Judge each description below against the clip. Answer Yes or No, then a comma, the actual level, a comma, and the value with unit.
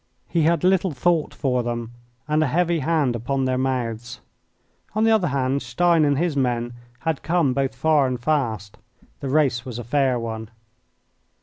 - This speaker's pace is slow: No, average, 175 wpm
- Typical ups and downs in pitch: Yes, average, 4.6 semitones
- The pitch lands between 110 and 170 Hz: Yes, low, 135 Hz